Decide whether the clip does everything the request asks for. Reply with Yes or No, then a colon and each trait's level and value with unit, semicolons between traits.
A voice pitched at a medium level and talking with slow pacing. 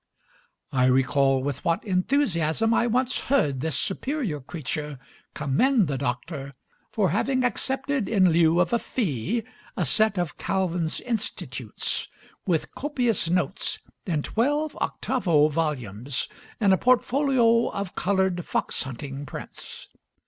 Yes: medium, 180 Hz; slow, 125 wpm